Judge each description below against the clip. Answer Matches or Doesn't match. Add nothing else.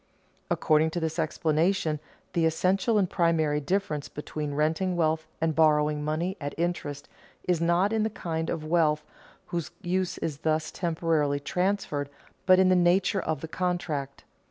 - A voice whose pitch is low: Doesn't match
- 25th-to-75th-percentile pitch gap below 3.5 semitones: Matches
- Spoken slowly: Doesn't match